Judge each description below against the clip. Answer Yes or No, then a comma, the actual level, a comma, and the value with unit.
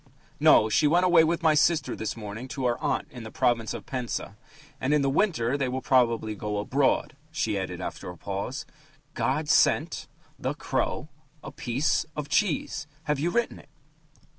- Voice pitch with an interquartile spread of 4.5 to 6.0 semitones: Yes, wide, 5.6 semitones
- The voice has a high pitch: No, low, 135 Hz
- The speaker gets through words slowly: No, average, 180 wpm